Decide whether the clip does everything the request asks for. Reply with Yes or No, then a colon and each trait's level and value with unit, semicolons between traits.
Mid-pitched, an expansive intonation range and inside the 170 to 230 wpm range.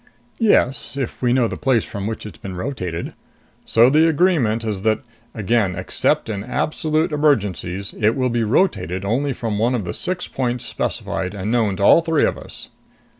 No: low, 115 Hz; wide, 5.7 semitones; average, 180 wpm